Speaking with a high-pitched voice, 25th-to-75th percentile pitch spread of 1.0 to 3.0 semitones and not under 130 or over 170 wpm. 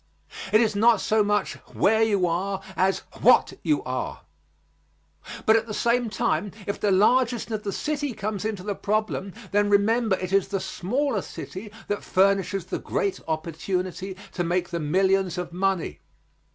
Yes: high, 200 Hz; narrow, 2.6 semitones; average, 165 wpm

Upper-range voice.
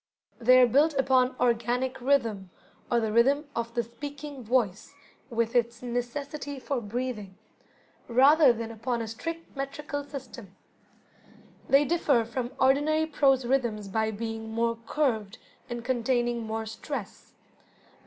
Yes: high, 245 Hz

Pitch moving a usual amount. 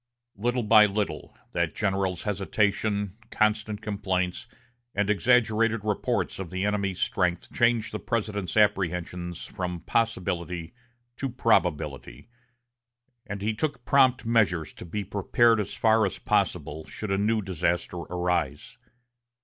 Yes: average, 3.4 semitones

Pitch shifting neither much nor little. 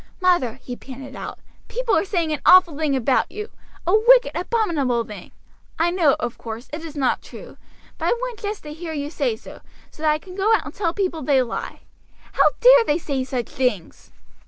No: wide, 6.8 semitones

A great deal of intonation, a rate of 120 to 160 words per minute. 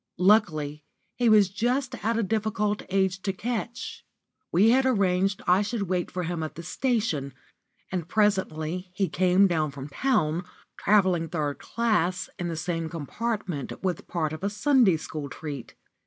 No: average, 4.7 semitones; average, 155 wpm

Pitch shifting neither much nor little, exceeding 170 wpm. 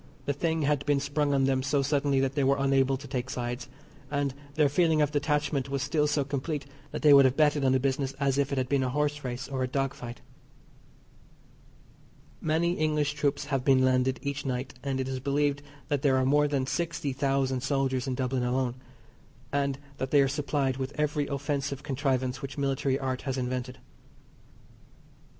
No: narrow, 1.7 semitones; average, 195 wpm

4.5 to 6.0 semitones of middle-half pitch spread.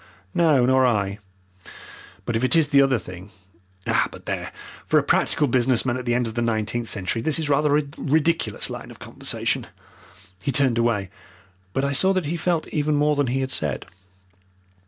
No: average, 4.0 semitones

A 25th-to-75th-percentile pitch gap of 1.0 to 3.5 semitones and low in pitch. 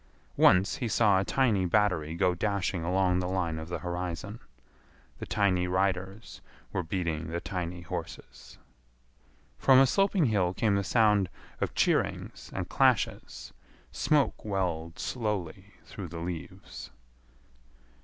Yes: average, 3.1 semitones; very low, 95 Hz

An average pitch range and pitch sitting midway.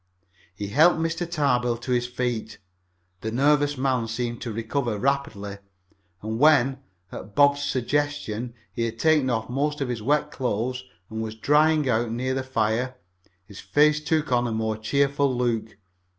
No: average, 4.2 semitones; low, 125 Hz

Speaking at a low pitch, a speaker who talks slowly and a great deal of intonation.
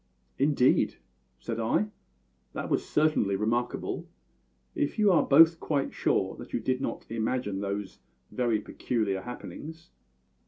Yes: low, 125 Hz; slow, 120 wpm; wide, 5.8 semitones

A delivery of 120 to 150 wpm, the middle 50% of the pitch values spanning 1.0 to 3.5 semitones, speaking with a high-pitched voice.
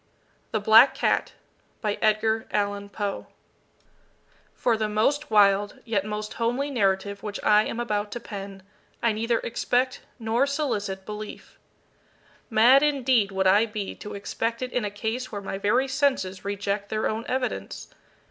Yes: average, 140 wpm; average, 2.9 semitones; high, 215 Hz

